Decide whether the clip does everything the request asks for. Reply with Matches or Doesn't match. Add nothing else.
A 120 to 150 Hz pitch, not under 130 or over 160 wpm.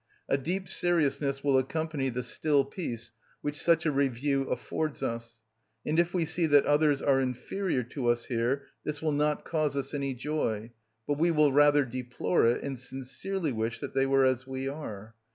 Doesn't match